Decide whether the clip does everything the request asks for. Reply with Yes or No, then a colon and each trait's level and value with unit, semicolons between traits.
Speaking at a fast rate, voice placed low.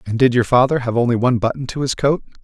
Yes: fast, 270 wpm; low, 125 Hz